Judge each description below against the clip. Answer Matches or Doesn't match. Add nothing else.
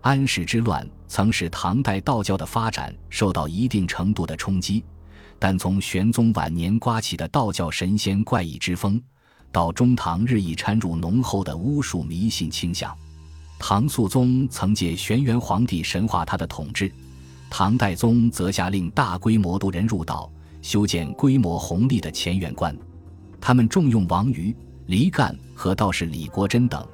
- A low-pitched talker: Matches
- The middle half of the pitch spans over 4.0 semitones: Matches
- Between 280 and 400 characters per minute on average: Doesn't match